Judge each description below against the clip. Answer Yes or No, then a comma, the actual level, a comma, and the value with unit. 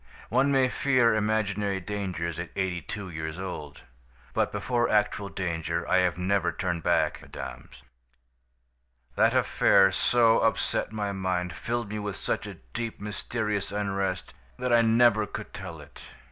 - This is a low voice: Yes, low, 100 Hz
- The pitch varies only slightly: No, average, 3.3 semitones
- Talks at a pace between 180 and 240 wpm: No, average, 145 wpm